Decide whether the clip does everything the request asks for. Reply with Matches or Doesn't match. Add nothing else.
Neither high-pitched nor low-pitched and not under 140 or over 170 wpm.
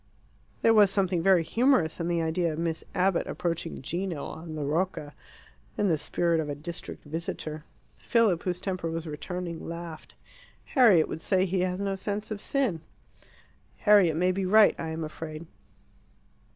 Matches